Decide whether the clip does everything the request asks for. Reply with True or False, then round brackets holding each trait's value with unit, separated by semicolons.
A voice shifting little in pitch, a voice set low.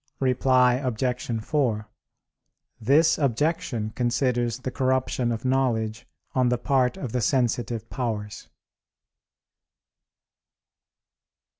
True (2.3 semitones; 125 Hz)